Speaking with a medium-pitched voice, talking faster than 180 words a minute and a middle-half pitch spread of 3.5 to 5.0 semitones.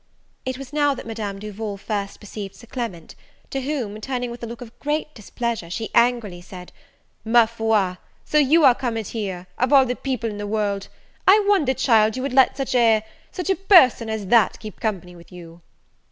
No: high, 230 Hz; average, 195 wpm; average, 4.1 semitones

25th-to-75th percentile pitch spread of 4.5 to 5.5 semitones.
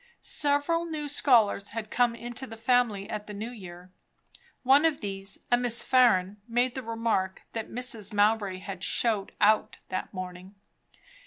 No: average, 3.8 semitones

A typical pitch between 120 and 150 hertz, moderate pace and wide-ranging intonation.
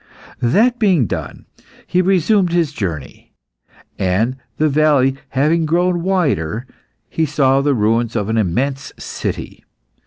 No: medium, 140 Hz; slow, 125 wpm; wide, 6.8 semitones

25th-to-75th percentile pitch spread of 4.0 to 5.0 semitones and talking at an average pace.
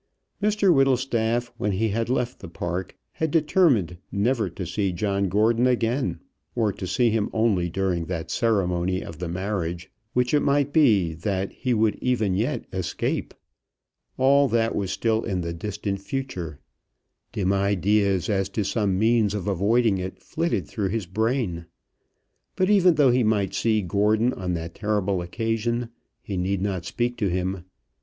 Yes: average, 4.3 semitones; average, 160 wpm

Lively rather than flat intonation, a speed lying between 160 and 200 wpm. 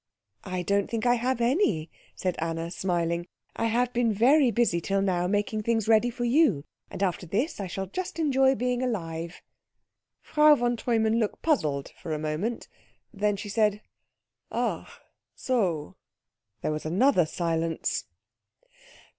No: wide, 5.9 semitones; average, 145 wpm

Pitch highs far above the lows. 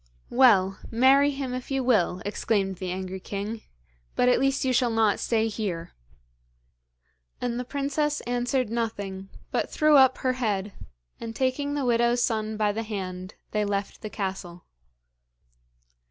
No: average, 4.4 semitones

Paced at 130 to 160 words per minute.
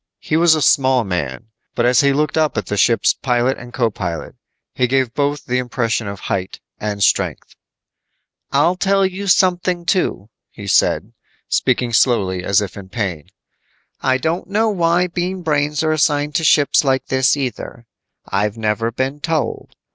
No: average, 170 wpm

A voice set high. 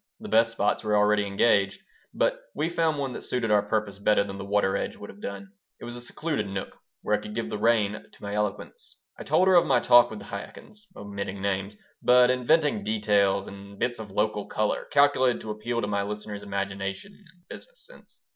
No: low, 105 Hz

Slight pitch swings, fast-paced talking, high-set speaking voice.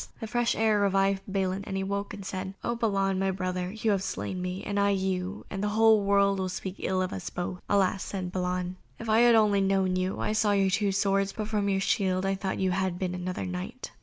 Yes: narrow, 1.5 semitones; fast, 240 wpm; high, 195 Hz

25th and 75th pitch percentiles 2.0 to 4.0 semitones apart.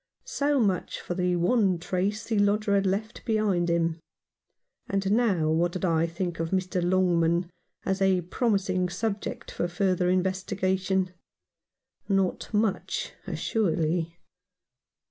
Yes: narrow, 2.5 semitones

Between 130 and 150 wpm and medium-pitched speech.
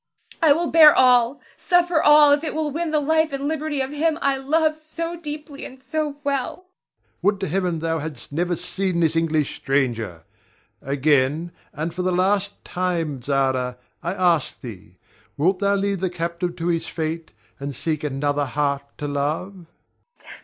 No: average, 170 wpm; medium, 180 Hz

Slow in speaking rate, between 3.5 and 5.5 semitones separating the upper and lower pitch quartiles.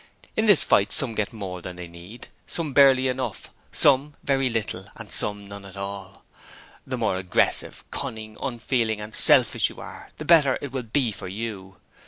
No: average, 180 wpm; average, 5.1 semitones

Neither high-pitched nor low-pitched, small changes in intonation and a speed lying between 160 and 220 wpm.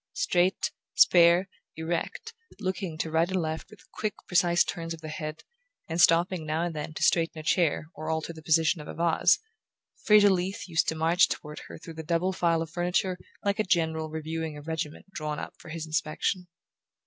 Yes: medium, 165 Hz; narrow, 2.1 semitones; average, 195 wpm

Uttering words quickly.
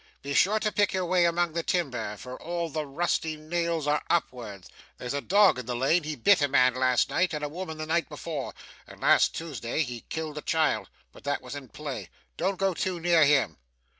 Yes: fast, 220 wpm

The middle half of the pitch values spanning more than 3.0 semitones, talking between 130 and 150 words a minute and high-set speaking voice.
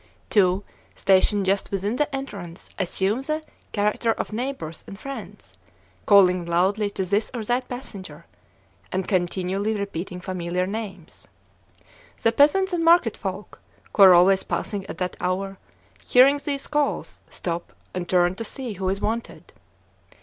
Yes: average, 4.2 semitones; average, 140 wpm; high, 200 Hz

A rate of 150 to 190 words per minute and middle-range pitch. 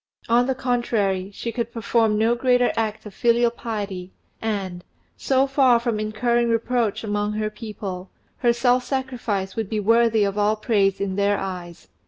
No: average, 165 wpm; high, 220 Hz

